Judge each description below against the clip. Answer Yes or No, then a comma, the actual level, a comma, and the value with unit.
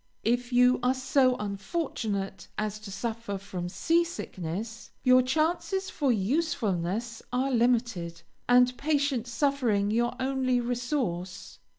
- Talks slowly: Yes, slow, 115 wpm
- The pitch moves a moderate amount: Yes, average, 4.4 semitones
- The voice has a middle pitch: No, high, 245 Hz